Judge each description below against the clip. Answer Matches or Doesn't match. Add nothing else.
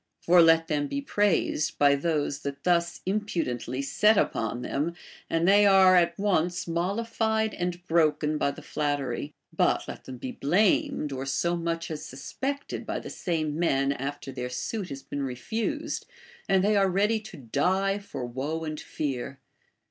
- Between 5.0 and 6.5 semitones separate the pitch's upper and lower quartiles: Matches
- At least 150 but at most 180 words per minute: Matches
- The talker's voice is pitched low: Doesn't match